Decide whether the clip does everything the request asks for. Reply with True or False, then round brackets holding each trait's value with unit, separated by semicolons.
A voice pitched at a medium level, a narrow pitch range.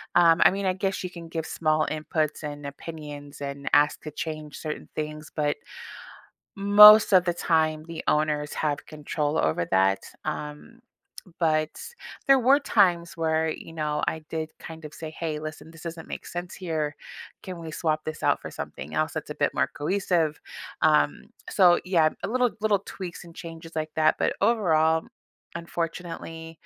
True (160 Hz; 2.3 semitones)